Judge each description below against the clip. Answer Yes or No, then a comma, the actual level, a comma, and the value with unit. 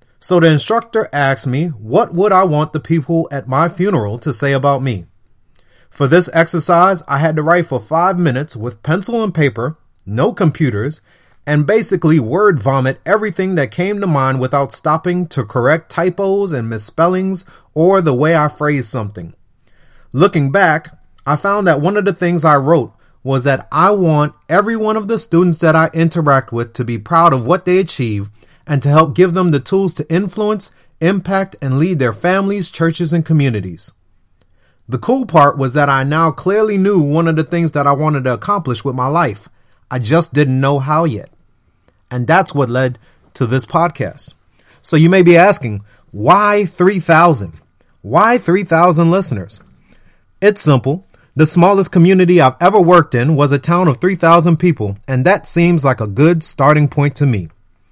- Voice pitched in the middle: Yes, medium, 155 Hz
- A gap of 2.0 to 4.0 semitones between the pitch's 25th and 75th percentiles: No, average, 5.2 semitones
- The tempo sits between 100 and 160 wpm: No, average, 180 wpm